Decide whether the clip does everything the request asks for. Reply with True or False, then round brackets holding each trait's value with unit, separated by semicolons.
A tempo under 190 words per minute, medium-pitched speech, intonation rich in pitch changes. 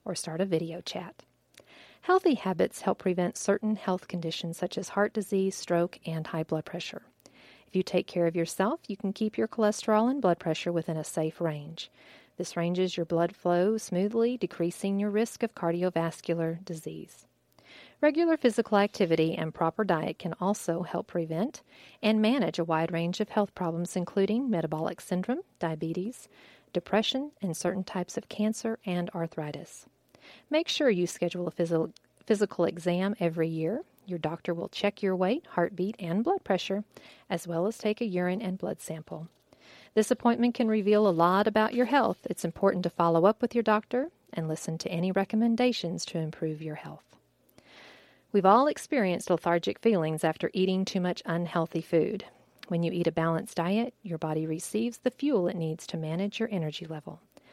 False (170 wpm; 180 Hz; 4.2 semitones)